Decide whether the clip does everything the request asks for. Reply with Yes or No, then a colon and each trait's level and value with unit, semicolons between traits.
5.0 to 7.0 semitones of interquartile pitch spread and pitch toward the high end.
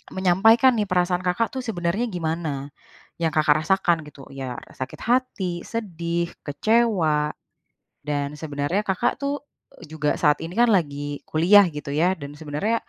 No: wide, 5.4 semitones; medium, 170 Hz